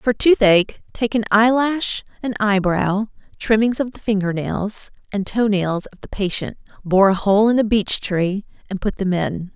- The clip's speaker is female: Yes, female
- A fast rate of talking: No, average, 180 wpm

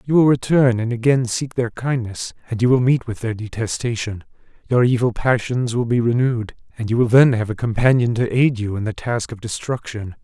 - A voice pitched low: Yes, low, 120 Hz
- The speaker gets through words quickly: Yes, fast, 210 wpm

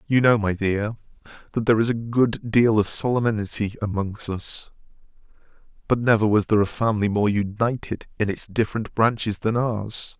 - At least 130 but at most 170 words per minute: Yes, average, 165 wpm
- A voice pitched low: Yes, low, 110 Hz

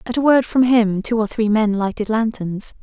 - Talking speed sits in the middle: No, fast, 235 wpm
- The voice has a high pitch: Yes, high, 220 Hz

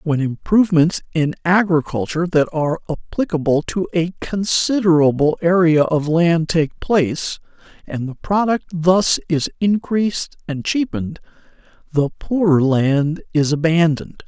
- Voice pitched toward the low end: No, medium, 165 Hz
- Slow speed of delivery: Yes, slow, 120 wpm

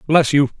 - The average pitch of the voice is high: No, medium, 145 Hz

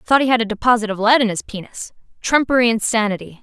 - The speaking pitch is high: Yes, high, 225 Hz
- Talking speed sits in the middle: No, fast, 210 wpm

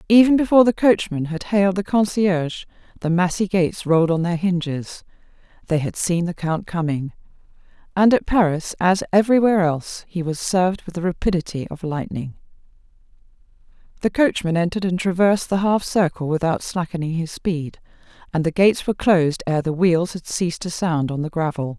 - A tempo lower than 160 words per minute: No, average, 170 wpm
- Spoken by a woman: Yes, female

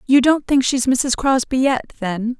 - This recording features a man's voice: No, female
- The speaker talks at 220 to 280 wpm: No, average, 200 wpm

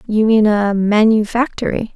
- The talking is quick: No, slow, 125 wpm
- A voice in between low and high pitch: No, high, 215 Hz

